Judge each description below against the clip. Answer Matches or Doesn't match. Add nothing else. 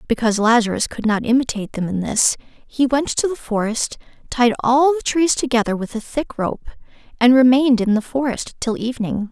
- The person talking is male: Doesn't match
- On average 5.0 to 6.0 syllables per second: Matches